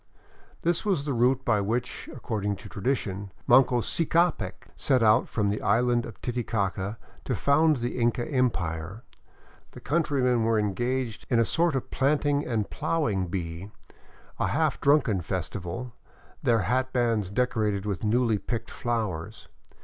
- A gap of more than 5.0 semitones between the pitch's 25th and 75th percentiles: No, average, 4.3 semitones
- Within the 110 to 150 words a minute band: Yes, average, 140 wpm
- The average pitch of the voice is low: Yes, low, 115 Hz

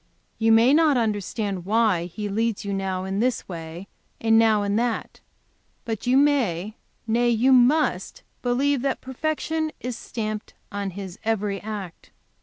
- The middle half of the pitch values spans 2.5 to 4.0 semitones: Yes, average, 3.7 semitones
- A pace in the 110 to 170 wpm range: Yes, average, 150 wpm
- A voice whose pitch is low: No, high, 220 Hz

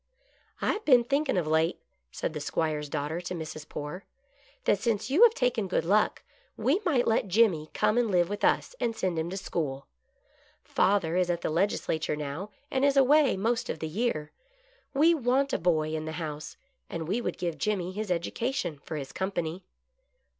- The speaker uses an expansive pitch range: Yes, wide, 7.2 semitones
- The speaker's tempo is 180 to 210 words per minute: Yes, average, 200 wpm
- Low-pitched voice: No, medium, 185 Hz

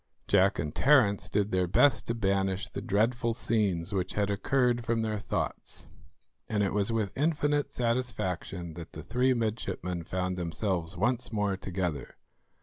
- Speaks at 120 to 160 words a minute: Yes, average, 150 wpm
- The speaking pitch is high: No, low, 105 Hz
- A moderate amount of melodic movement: Yes, average, 4.3 semitones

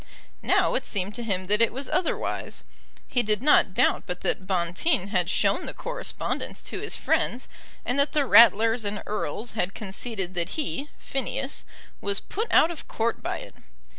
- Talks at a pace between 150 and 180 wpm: Yes, average, 175 wpm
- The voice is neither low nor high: No, high, 220 Hz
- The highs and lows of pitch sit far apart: Yes, wide, 5.8 semitones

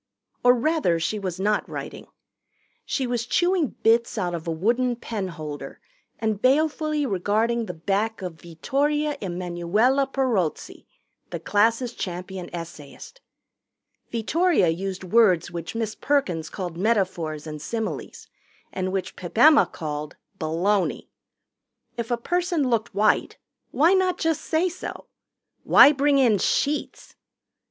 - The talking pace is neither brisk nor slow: No, slow, 130 wpm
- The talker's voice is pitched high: Yes, high, 220 Hz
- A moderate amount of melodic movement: No, wide, 7.3 semitones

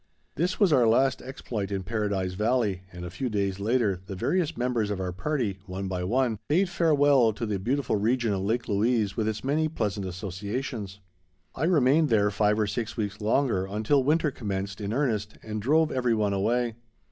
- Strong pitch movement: No, average, 4.7 semitones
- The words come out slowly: No, average, 190 wpm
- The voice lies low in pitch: Yes, low, 110 Hz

